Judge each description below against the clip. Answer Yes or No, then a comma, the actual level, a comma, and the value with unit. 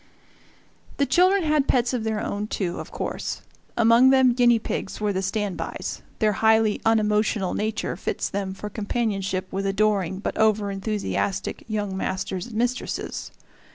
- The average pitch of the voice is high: Yes, high, 215 Hz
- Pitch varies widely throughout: No, average, 2.9 semitones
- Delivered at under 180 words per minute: Yes, average, 155 wpm